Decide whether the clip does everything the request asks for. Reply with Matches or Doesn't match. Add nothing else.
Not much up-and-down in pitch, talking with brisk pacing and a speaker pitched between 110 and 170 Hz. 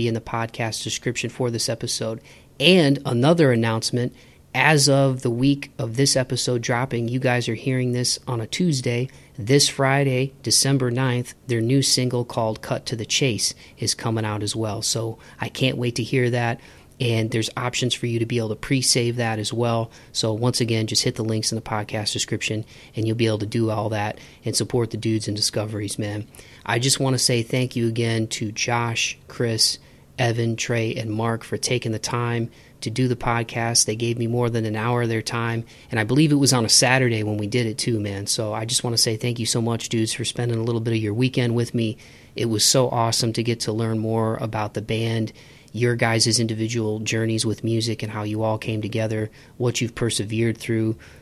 Matches